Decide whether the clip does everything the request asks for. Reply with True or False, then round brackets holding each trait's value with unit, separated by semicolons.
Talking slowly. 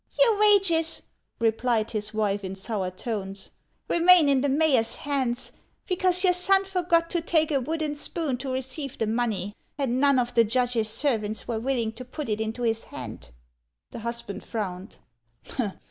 False (165 wpm)